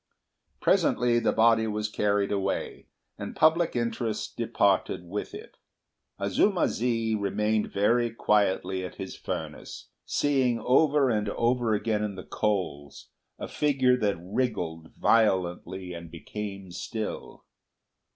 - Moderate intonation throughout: Yes, average, 3.6 semitones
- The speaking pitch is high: No, low, 105 Hz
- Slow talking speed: Yes, slow, 120 wpm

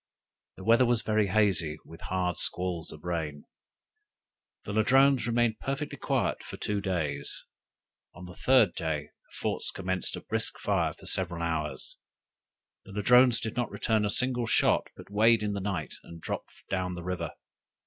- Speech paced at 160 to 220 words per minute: Yes, average, 165 wpm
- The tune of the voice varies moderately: Yes, average, 4.9 semitones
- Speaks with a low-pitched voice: Yes, very low, 95 Hz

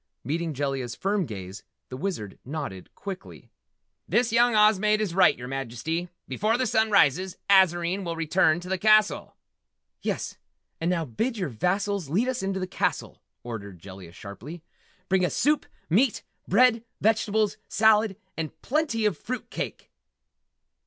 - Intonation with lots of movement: Yes, wide, 7.0 semitones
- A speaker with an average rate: Yes, average, 150 wpm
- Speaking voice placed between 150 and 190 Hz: Yes, medium, 185 Hz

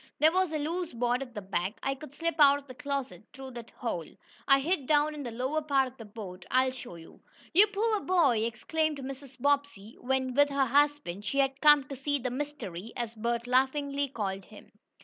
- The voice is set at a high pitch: Yes, very high, 270 Hz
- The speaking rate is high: Yes, fast, 210 wpm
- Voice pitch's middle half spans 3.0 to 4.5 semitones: Yes, average, 3.7 semitones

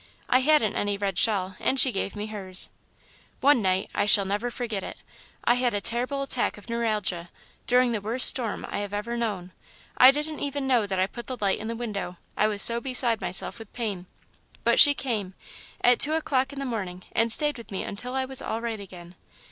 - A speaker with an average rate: No, fast, 215 wpm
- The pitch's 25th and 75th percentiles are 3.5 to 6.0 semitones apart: Yes, average, 4.1 semitones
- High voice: Yes, high, 225 Hz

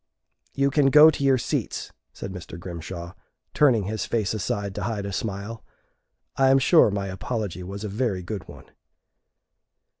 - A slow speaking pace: No, average, 160 wpm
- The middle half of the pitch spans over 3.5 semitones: Yes, average, 5.1 semitones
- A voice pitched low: Yes, low, 105 Hz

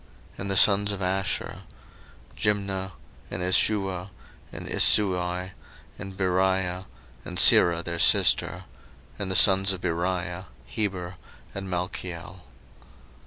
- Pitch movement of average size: No, narrow, 1.4 semitones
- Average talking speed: No, slow, 115 wpm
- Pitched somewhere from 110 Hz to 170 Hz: No, very low, 95 Hz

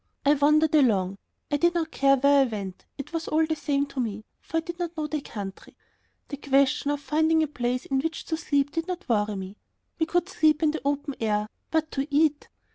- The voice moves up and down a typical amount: Yes, average, 3.5 semitones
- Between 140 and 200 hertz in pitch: No, very high, 290 Hz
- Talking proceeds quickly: Yes, fast, 225 wpm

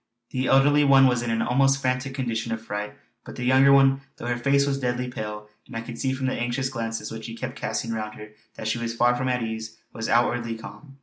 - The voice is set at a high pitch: No, low, 120 Hz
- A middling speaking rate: No, fast, 245 wpm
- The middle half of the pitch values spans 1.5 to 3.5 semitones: Yes, average, 2.7 semitones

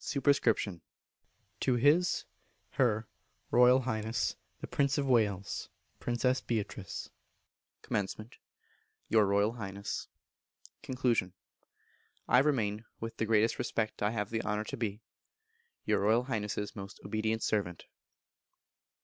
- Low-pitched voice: Yes, low, 110 Hz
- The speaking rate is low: Yes, slow, 110 wpm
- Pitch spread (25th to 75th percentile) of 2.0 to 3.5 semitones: Yes, average, 3.2 semitones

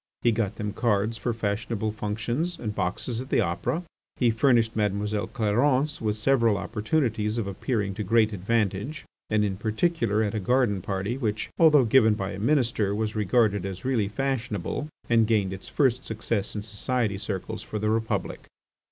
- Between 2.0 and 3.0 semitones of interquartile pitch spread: Yes, average, 2.7 semitones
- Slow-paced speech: No, average, 170 wpm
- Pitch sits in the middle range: No, low, 110 Hz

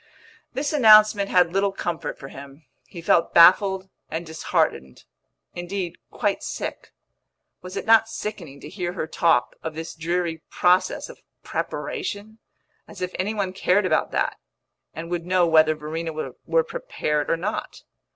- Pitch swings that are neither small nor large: Yes, average, 3.8 semitones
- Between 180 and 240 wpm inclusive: No, average, 150 wpm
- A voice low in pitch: No, medium, 180 Hz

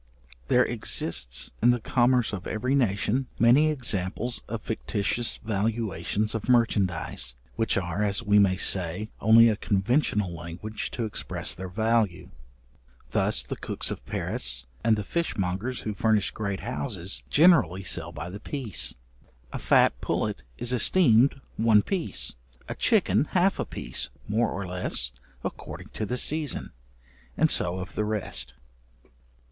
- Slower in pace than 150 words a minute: Yes, average, 140 wpm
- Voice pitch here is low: Yes, low, 105 Hz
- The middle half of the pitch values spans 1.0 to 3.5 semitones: No, average, 4.2 semitones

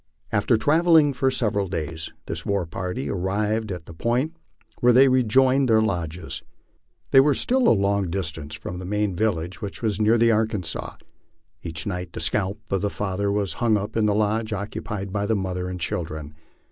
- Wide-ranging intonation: No, average, 3.7 semitones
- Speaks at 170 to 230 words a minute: Yes, average, 185 wpm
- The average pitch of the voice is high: No, low, 100 Hz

